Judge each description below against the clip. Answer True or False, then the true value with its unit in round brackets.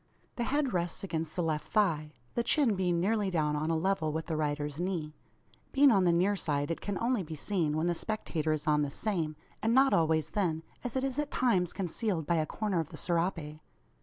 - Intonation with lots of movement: False (4.9 semitones)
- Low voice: False (170 Hz)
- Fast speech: True (220 wpm)